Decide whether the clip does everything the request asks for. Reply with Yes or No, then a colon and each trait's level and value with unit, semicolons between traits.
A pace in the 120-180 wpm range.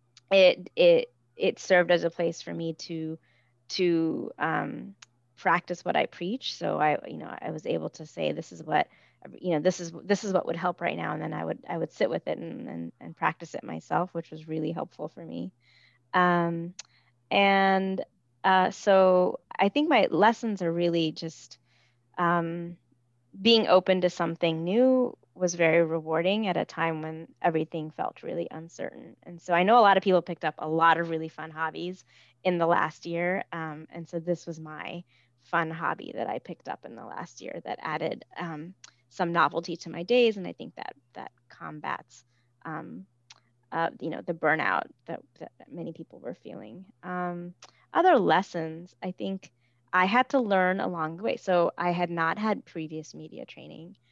No: average, 190 wpm